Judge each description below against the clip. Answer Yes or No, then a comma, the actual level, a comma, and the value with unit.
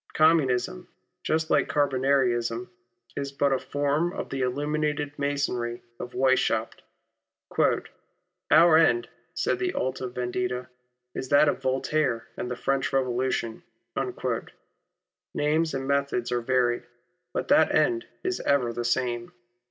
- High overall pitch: No, low, 135 Hz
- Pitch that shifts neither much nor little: Yes, average, 3.2 semitones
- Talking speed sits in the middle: No, slow, 125 wpm